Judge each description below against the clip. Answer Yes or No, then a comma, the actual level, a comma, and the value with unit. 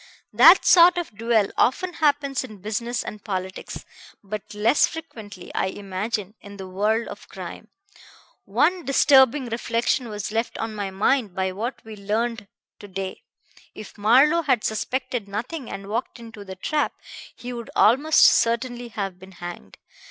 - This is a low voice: No, high, 225 Hz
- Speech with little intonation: No, average, 4.2 semitones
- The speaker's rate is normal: Yes, average, 150 wpm